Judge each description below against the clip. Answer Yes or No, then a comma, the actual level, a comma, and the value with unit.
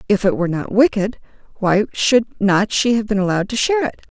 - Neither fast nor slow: No, fast, 215 wpm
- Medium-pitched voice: No, high, 210 Hz